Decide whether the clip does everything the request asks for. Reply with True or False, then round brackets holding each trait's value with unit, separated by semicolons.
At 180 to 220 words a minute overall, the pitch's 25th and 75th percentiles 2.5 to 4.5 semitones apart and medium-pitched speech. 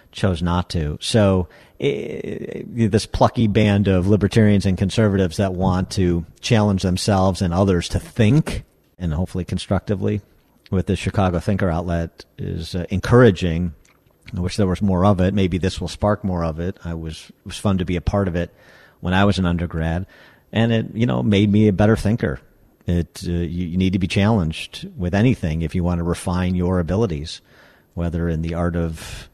False (190 wpm; 2.8 semitones; 95 Hz)